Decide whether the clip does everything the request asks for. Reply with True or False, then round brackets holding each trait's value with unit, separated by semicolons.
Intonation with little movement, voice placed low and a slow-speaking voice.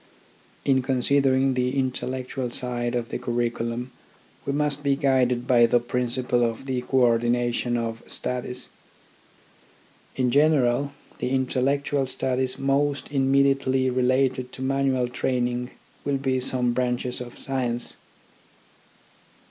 True (1.7 semitones; 130 Hz; 115 wpm)